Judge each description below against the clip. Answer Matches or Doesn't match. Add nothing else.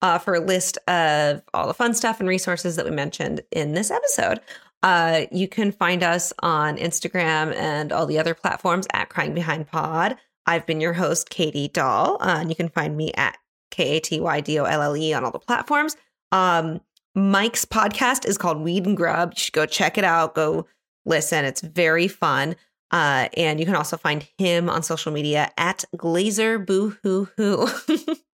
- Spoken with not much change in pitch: Doesn't match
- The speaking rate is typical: Matches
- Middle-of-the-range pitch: Matches